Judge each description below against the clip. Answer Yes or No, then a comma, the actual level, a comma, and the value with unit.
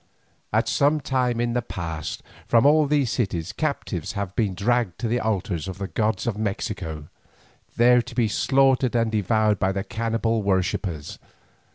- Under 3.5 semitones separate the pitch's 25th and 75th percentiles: No, average, 4.1 semitones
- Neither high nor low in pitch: No, low, 110 Hz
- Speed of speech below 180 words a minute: Yes, average, 165 wpm